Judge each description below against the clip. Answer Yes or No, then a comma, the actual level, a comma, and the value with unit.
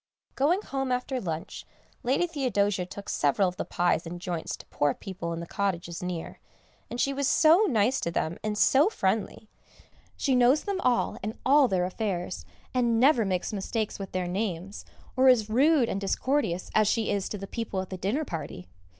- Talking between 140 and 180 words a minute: No, average, 190 wpm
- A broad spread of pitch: Yes, wide, 6.1 semitones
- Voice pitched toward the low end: No, high, 210 Hz